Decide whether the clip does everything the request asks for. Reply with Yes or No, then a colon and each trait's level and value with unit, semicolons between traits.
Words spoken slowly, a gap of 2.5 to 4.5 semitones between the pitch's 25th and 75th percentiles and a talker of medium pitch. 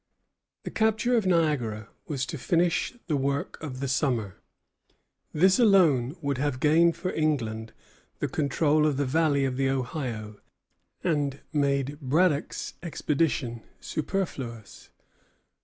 Yes: slow, 125 wpm; average, 4.1 semitones; medium, 145 Hz